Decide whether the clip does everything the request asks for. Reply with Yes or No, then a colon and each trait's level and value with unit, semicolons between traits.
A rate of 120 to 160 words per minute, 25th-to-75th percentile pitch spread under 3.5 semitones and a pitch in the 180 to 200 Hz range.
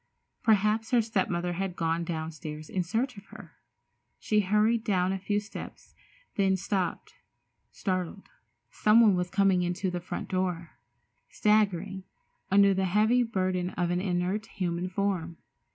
Yes: average, 140 wpm; average, 2.9 semitones; high, 190 Hz